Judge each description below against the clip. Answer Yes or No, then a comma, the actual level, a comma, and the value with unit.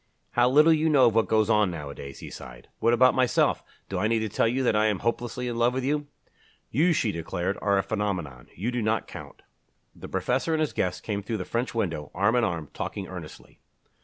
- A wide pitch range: No, average, 4.4 semitones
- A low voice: Yes, low, 110 Hz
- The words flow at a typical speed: No, fast, 225 wpm